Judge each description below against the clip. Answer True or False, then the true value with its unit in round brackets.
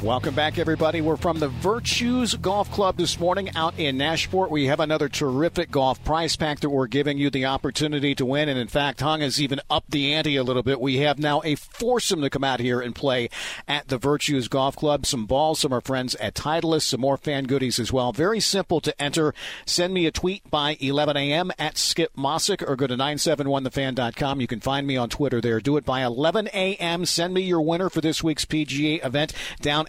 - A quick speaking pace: True (220 wpm)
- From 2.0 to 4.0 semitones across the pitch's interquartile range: True (2.9 semitones)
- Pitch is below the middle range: False (150 Hz)